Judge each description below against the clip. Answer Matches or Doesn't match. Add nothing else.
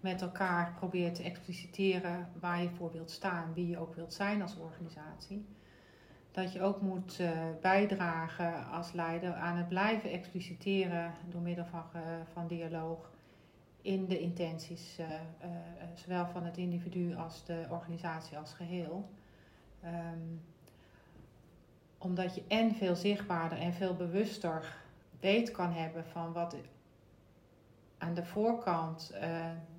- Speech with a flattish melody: Matches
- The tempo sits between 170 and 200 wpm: Doesn't match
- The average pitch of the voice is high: Doesn't match